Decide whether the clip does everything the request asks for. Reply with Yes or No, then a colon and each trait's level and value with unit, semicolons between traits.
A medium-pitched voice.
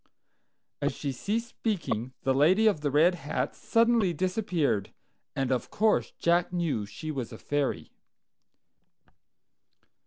Yes: medium, 160 Hz